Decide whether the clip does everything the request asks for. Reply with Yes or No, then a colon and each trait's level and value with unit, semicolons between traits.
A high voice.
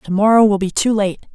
Yes: high, 205 Hz